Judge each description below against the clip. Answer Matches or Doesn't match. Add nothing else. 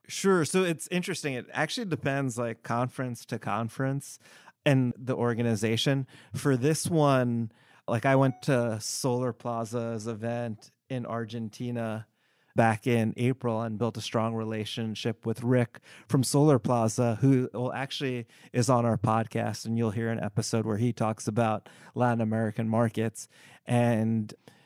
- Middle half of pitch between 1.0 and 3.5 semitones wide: Matches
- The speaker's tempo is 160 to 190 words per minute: Doesn't match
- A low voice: Matches